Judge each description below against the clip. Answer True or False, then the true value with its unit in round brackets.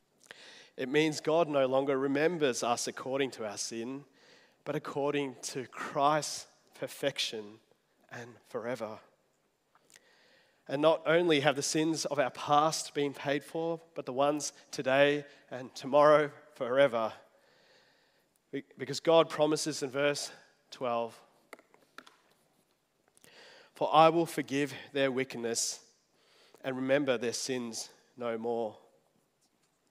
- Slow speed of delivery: True (110 wpm)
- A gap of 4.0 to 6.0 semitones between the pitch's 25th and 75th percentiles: False (2.5 semitones)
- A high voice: False (140 Hz)